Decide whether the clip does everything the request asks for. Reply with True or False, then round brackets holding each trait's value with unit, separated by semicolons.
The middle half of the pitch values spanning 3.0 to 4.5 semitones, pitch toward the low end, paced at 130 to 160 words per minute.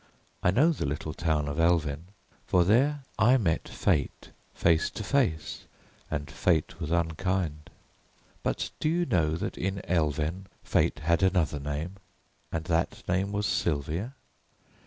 True (4.0 semitones; 85 Hz; 140 wpm)